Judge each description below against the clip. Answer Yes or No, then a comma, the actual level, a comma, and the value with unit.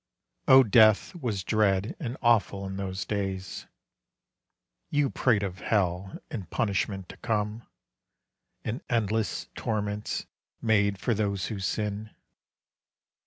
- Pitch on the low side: Yes, low, 105 Hz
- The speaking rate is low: Yes, slow, 115 wpm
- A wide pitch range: No, narrow, 2.4 semitones